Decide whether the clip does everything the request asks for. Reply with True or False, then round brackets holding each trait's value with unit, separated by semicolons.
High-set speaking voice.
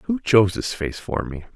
False (105 Hz)